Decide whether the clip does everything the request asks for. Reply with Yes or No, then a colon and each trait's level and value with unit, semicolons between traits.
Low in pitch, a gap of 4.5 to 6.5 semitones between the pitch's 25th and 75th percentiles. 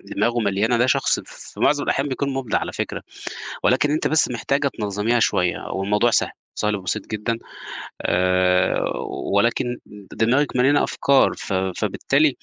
Yes: low, 115 Hz; average, 4.8 semitones